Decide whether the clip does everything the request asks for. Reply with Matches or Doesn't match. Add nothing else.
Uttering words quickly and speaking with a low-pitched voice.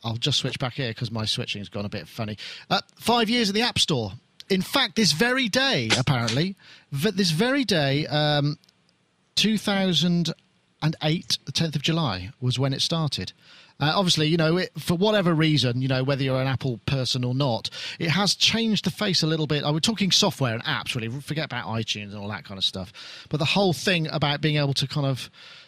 Doesn't match